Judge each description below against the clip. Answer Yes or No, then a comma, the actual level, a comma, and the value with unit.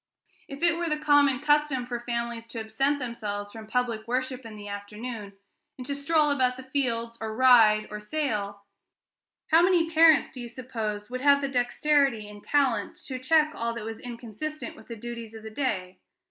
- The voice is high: Yes, high, 245 Hz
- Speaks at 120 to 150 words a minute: No, average, 190 wpm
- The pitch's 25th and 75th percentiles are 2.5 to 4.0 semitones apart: No, average, 4.4 semitones